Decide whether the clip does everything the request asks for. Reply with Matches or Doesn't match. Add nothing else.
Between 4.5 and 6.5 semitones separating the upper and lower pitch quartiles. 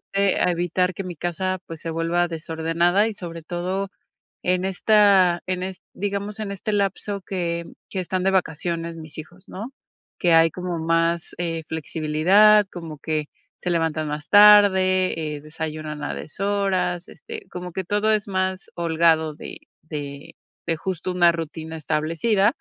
Doesn't match